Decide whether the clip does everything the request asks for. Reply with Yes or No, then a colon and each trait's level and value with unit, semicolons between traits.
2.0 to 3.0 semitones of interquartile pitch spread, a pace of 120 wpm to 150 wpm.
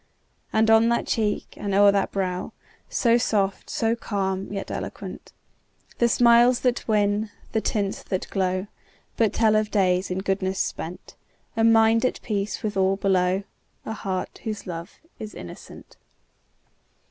Yes: average, 2.7 semitones; average, 145 wpm